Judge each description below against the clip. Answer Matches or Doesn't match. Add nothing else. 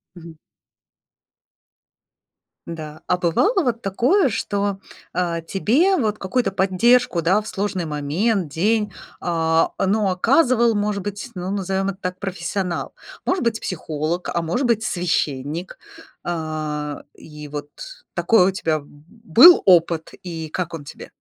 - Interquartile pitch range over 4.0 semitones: Matches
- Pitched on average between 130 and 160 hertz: Doesn't match